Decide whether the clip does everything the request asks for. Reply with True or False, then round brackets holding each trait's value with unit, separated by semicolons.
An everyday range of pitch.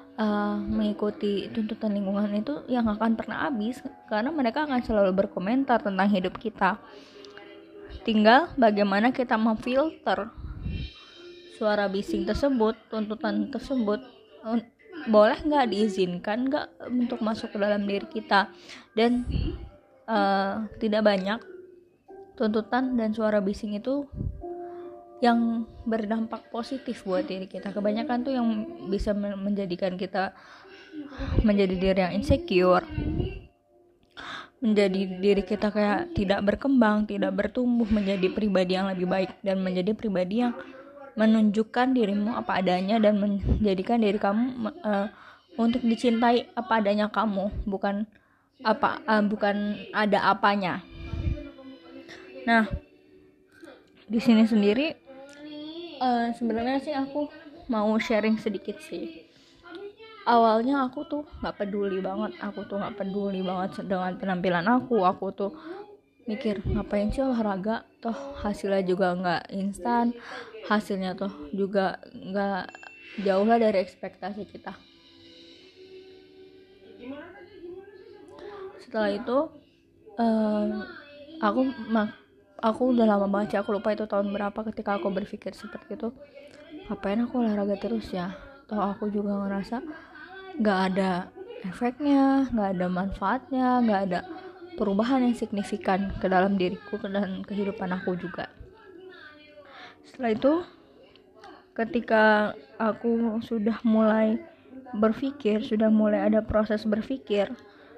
True (4.2 semitones)